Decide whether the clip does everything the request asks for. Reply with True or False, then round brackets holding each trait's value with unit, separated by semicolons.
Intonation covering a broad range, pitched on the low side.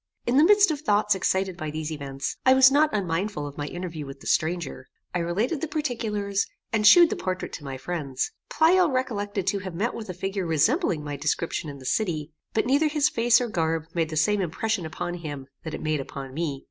False (6.9 semitones; 185 Hz)